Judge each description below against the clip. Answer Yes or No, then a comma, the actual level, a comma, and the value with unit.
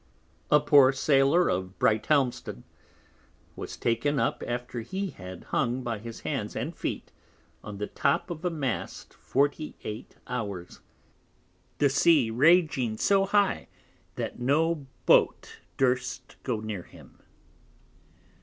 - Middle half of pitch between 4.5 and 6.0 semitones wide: Yes, average, 5.1 semitones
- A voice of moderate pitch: No, low, 130 Hz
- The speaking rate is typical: No, slow, 120 wpm